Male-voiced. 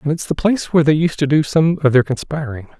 Yes: male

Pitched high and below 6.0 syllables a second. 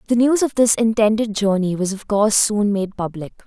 Yes: high, 210 Hz; 5.4 syllables/s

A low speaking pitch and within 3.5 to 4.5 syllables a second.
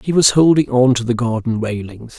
No: low, 125 Hz; 5.3 syllables/s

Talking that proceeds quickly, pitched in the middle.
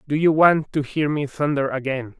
Yes: fast, 220 wpm; medium, 145 Hz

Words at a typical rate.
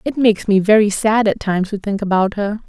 No: fast, 245 wpm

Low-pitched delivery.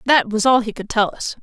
No: high, 230 Hz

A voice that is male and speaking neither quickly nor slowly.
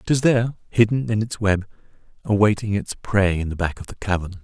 Yes: male; average, 190 wpm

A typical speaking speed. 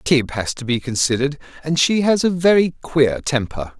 Yes: average, 190 wpm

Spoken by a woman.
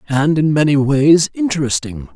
No: male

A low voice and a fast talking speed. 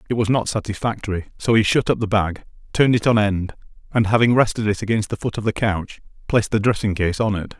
Yes: low, 105 Hz; fast, 235 wpm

